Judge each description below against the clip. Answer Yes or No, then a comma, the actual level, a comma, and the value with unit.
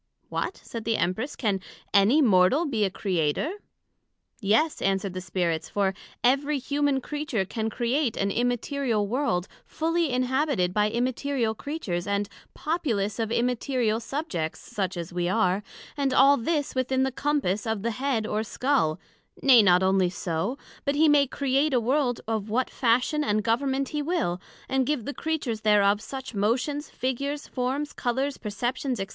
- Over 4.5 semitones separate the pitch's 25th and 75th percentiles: Yes, wide, 5.6 semitones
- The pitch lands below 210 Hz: No, high, 240 Hz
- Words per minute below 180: Yes, average, 160 wpm